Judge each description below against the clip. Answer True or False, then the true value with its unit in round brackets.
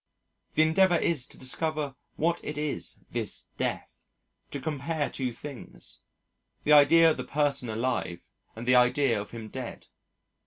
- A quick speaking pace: False (150 wpm)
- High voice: False (140 Hz)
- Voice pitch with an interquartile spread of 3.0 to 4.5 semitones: True (4.0 semitones)